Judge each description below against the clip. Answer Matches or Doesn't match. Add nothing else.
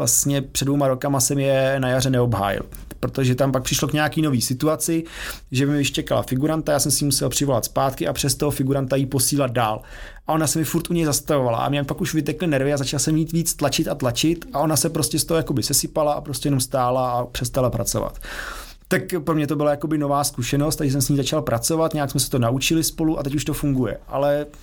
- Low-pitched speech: Doesn't match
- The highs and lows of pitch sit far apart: Doesn't match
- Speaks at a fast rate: Matches